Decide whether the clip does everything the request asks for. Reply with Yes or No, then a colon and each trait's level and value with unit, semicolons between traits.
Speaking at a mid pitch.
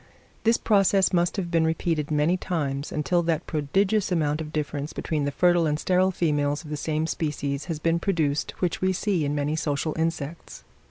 Yes: medium, 160 Hz